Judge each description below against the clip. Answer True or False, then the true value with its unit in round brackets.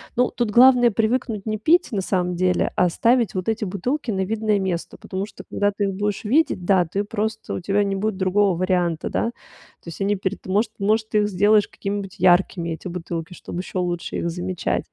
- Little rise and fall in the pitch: False (3.0 semitones)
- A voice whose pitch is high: True (200 Hz)